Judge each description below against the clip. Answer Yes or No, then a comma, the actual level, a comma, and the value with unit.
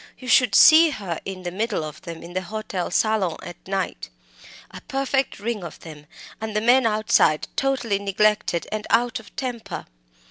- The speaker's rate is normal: Yes, average, 175 wpm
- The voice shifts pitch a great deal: No, average, 4.8 semitones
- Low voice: No, high, 210 Hz